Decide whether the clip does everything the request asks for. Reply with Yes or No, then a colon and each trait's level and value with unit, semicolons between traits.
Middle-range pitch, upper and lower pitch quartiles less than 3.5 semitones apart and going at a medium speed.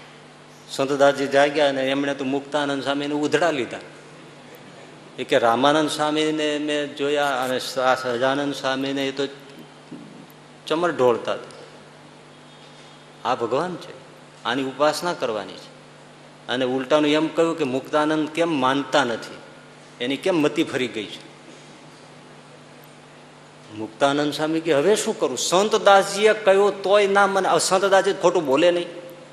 No: medium, 145 Hz; average, 3.9 semitones; average, 115 wpm